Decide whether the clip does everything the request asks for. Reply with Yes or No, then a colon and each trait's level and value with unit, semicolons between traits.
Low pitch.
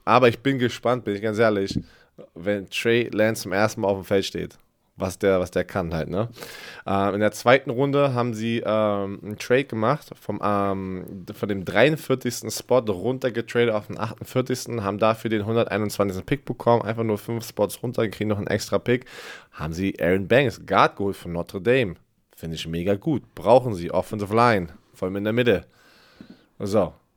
Yes: low, 105 Hz